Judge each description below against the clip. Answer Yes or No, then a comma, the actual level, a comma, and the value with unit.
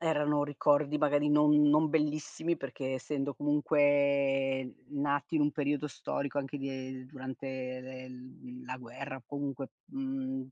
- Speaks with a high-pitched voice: No, medium, 140 Hz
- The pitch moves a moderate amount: No, narrow, 2.0 semitones